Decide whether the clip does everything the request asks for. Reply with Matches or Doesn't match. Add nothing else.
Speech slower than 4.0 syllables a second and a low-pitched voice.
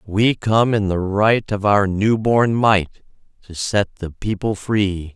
Matches